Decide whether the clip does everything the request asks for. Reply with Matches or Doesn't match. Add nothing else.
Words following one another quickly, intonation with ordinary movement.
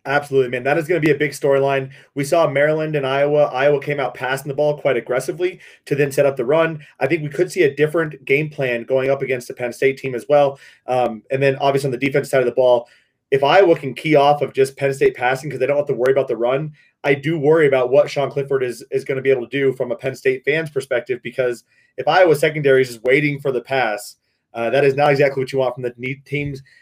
Doesn't match